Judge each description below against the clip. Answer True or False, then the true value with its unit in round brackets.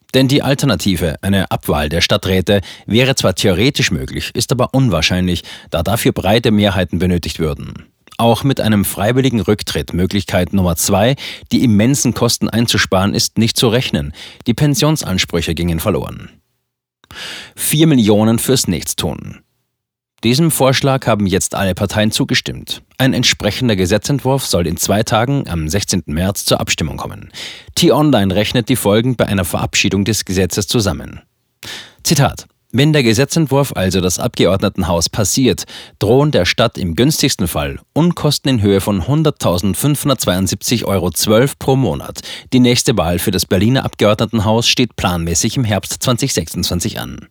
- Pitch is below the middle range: True (105 Hz)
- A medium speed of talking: True (140 wpm)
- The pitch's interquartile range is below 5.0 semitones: False (5.3 semitones)